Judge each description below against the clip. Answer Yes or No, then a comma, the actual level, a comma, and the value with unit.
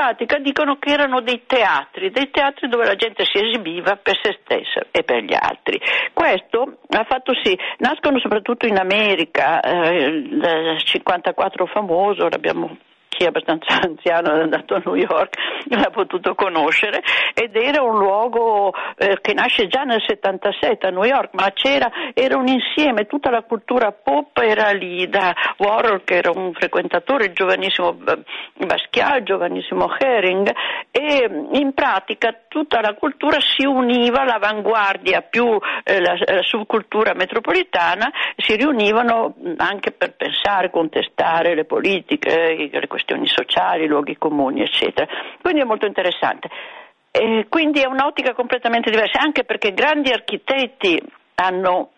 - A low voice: No, high, 230 Hz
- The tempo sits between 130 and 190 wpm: Yes, average, 140 wpm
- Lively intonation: Yes, wide, 6.2 semitones